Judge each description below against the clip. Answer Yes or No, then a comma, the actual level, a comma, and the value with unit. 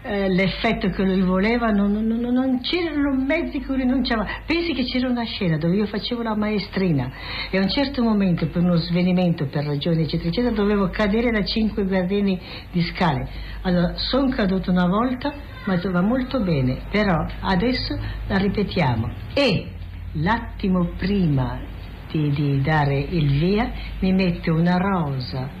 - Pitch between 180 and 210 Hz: Yes, high, 190 Hz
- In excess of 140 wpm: Yes, average, 155 wpm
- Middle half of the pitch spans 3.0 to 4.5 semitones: No, average, 5.3 semitones